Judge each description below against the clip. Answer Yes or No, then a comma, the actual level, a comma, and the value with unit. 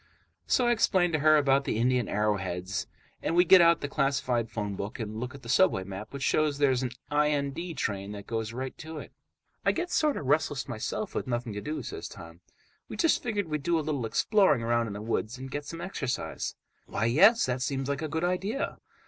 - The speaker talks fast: Yes, fast, 220 wpm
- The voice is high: No, medium, 140 Hz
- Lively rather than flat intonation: Yes, wide, 5.7 semitones